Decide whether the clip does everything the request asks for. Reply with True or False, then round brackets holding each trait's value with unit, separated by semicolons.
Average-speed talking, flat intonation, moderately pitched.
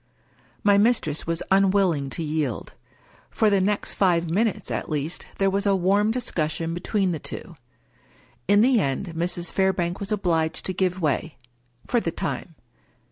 False (160 wpm; 3.7 semitones; 180 Hz)